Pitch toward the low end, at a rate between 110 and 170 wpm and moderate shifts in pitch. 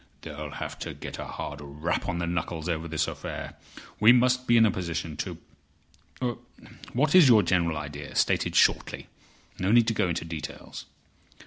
No: very low, 85 Hz; average, 165 wpm; wide, 6.5 semitones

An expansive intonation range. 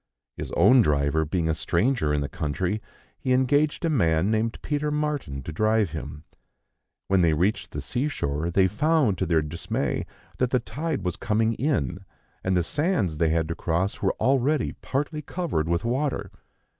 Yes: wide, 8.7 semitones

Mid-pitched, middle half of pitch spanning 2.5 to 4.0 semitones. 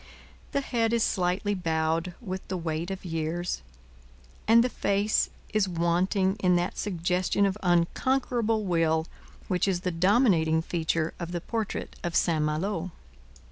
Yes: medium, 180 Hz; average, 3.4 semitones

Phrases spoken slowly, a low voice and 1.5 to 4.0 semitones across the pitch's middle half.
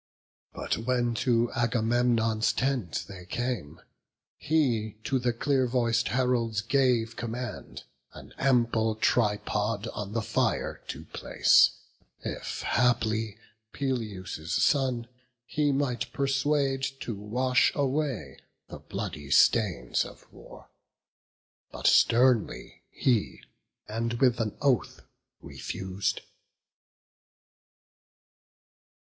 Yes: slow, 95 wpm; low, 120 Hz; average, 2.9 semitones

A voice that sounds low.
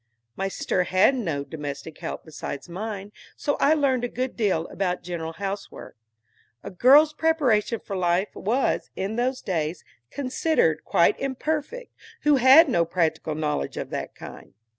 No: high, 200 Hz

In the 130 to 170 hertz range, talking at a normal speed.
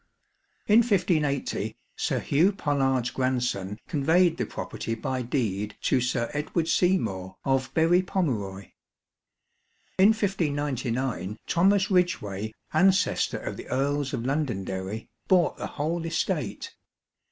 No: medium, 140 Hz; slow, 110 wpm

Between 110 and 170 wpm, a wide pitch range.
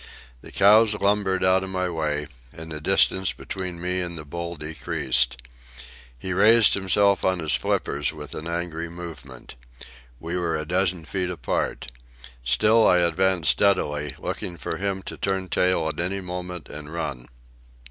No: average, 160 wpm; average, 3.1 semitones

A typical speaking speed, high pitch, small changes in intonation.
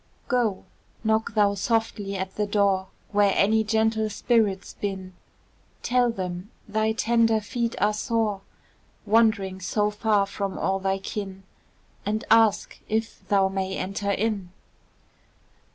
No: slow, 125 wpm; high, 210 Hz; narrow, 2.3 semitones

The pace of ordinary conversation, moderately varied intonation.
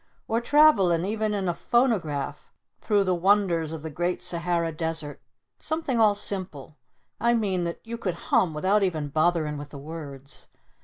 Yes: average, 160 wpm; average, 4.7 semitones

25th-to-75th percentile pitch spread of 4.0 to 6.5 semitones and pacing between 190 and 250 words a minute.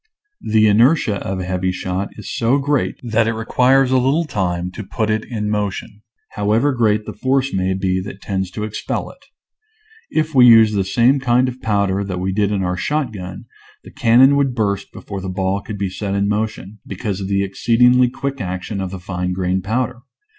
Yes: average, 4.3 semitones; fast, 205 wpm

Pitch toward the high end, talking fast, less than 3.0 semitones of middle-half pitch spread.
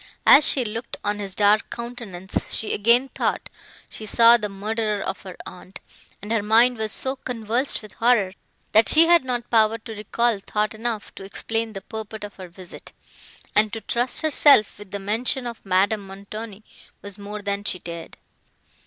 No: high, 215 Hz; average, 180 wpm; narrow, 2.6 semitones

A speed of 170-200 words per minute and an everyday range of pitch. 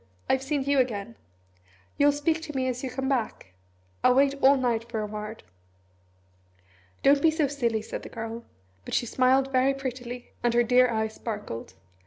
Yes: average, 180 wpm; average, 3.2 semitones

